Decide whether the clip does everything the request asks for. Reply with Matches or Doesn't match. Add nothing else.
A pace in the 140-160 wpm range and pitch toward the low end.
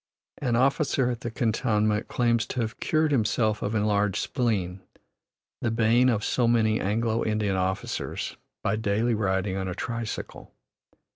Matches